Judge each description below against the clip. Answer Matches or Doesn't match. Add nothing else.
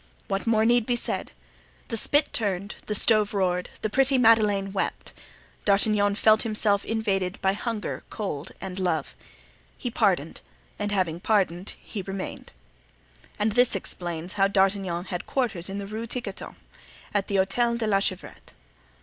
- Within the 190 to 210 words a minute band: Doesn't match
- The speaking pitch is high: Matches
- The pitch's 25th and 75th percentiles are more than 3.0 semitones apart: Doesn't match